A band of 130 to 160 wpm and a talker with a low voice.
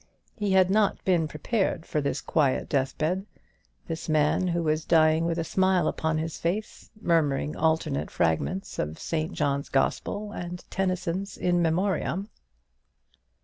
No: average, 140 wpm; medium, 165 Hz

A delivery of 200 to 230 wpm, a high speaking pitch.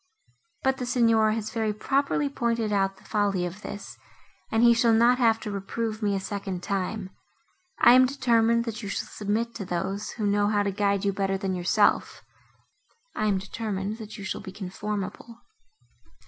No: average, 175 wpm; high, 210 Hz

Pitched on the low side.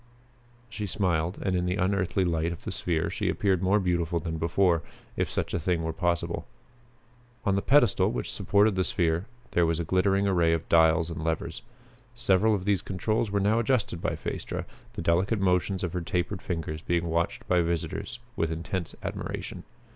Yes: very low, 90 Hz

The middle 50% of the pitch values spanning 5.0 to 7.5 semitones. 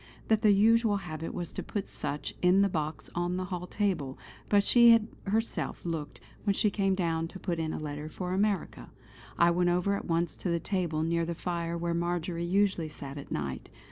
No: average, 3.3 semitones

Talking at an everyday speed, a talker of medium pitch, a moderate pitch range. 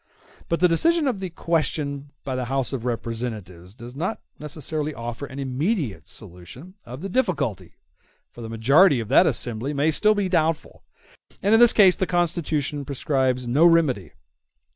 No: average, 165 wpm; medium, 145 Hz; wide, 6.0 semitones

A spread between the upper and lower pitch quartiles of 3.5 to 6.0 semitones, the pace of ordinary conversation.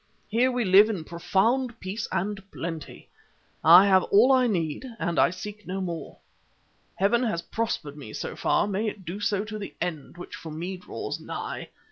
Yes: average, 3.8 semitones; average, 175 wpm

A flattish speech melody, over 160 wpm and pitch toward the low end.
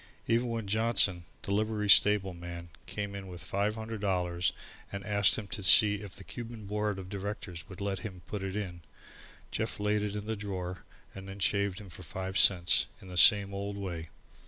Yes: narrow, 2.1 semitones; average, 200 wpm; low, 100 Hz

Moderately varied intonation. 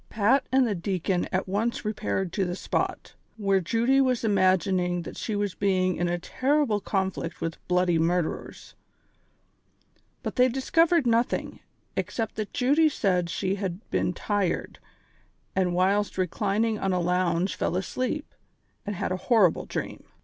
Yes: average, 4.1 semitones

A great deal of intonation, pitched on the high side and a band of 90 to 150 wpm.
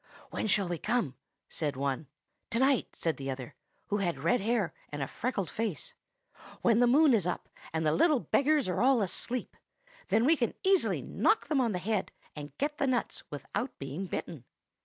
No: wide, 8.0 semitones; high, 215 Hz; average, 190 wpm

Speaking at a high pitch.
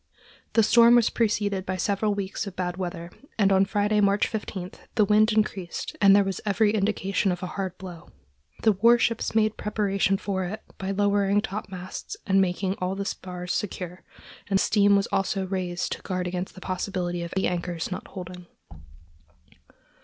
Yes: high, 195 Hz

